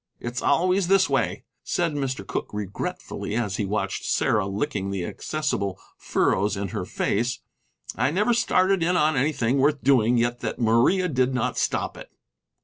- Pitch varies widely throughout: Yes, wide, 6.8 semitones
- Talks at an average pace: Yes, average, 160 wpm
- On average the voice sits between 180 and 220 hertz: No, low, 125 Hz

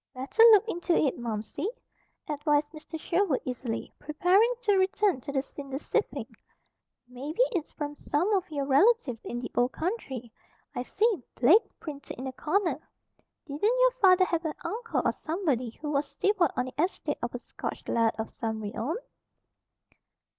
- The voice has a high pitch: Yes, very high, 300 Hz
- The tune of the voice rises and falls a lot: Yes, wide, 6.6 semitones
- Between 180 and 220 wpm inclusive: No, average, 160 wpm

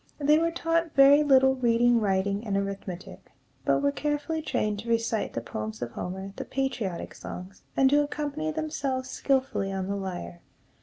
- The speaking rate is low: No, average, 165 wpm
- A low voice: No, high, 230 Hz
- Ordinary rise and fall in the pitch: No, wide, 7.1 semitones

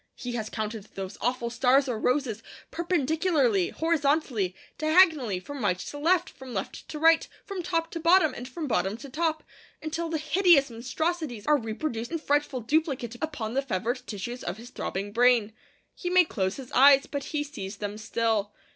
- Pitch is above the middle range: Yes, very high, 265 Hz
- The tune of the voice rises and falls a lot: Yes, wide, 6.0 semitones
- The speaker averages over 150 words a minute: Yes, average, 175 wpm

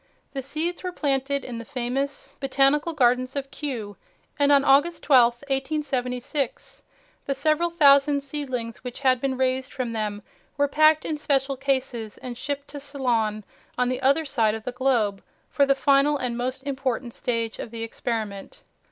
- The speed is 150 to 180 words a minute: Yes, average, 165 wpm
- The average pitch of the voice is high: Yes, very high, 270 Hz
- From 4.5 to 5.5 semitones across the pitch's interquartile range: No, average, 2.7 semitones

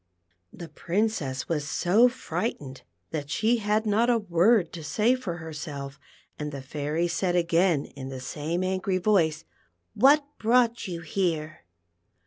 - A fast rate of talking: No, average, 150 wpm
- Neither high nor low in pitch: Yes, medium, 175 Hz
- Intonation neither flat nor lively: No, wide, 6.1 semitones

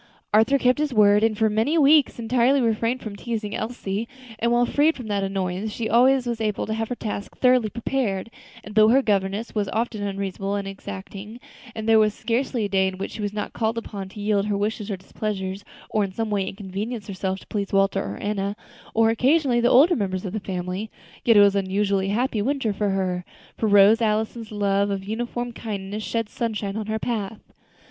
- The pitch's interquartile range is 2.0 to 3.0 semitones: Yes, average, 2.7 semitones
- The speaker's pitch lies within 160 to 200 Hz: No, high, 215 Hz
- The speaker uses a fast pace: Yes, fast, 215 wpm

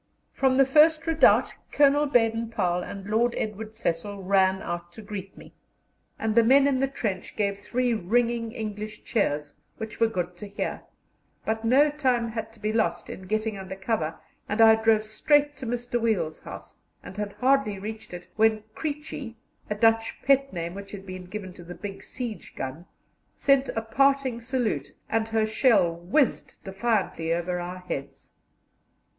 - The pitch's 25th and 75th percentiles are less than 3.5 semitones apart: No, average, 4.1 semitones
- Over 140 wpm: Yes, average, 170 wpm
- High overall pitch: Yes, high, 220 Hz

